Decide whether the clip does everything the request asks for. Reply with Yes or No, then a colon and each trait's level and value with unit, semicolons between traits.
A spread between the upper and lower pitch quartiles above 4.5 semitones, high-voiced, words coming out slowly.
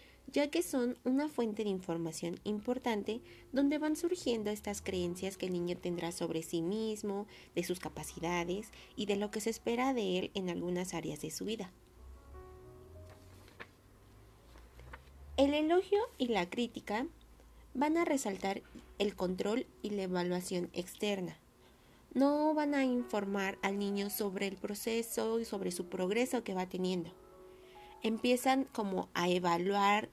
No: wide, 5.5 semitones; high, 200 Hz; average, 140 wpm